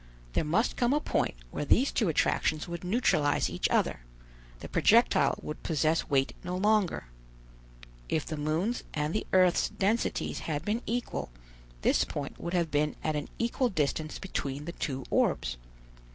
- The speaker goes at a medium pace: Yes, average, 160 wpm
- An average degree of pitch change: No, wide, 6.0 semitones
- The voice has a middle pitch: Yes, medium, 165 Hz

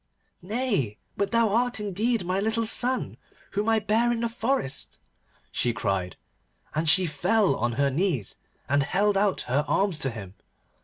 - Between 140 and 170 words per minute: Yes, average, 160 wpm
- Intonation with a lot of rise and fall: Yes, wide, 8.1 semitones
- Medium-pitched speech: No, high, 195 Hz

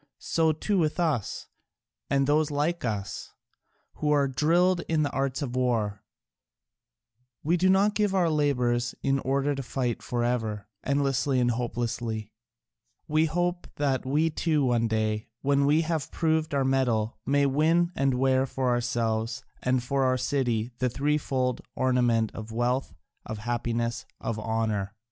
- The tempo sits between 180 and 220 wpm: No, average, 150 wpm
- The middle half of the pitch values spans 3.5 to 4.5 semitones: Yes, average, 4.0 semitones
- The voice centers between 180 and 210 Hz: No, low, 130 Hz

